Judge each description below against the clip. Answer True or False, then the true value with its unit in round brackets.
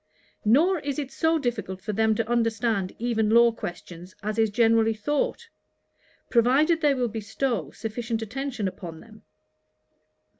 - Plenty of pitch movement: False (3.5 semitones)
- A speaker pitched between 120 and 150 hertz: False (230 Hz)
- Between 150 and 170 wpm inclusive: False (140 wpm)